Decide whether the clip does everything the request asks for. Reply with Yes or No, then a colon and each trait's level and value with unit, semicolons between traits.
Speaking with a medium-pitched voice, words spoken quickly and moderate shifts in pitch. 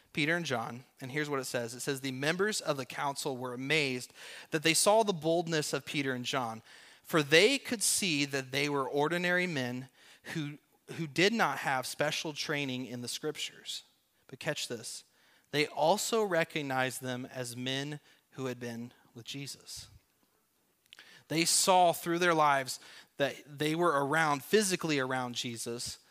No: medium, 145 Hz; average, 165 wpm; average, 4.1 semitones